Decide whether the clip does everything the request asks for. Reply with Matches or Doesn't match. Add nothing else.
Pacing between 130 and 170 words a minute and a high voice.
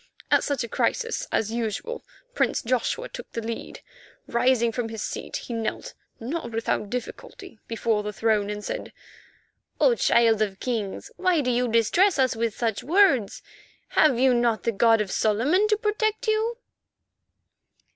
Matches